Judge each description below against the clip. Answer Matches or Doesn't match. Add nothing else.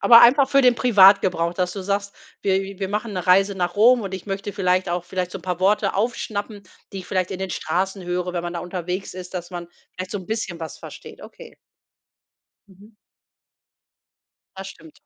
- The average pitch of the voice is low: Doesn't match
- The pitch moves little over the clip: Matches